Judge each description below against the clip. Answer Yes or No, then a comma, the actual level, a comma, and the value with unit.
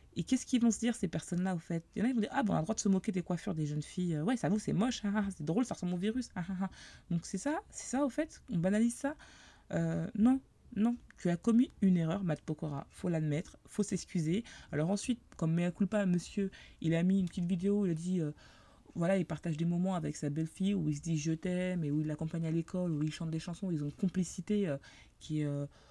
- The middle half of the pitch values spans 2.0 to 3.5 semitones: No, average, 4.3 semitones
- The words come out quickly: Yes, fast, 280 wpm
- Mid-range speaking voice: Yes, medium, 180 Hz